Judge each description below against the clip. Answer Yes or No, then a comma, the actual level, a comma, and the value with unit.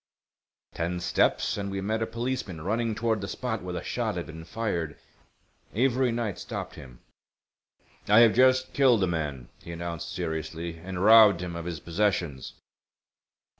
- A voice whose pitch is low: Yes, very low, 95 Hz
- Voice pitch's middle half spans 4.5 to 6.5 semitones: Yes, average, 5.2 semitones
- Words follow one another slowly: No, average, 160 wpm